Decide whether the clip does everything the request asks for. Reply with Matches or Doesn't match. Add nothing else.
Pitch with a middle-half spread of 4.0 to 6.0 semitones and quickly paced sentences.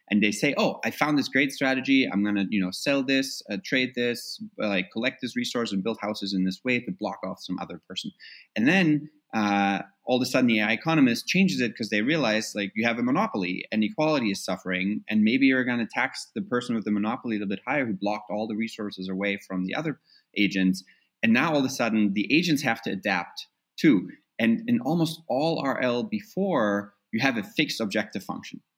Matches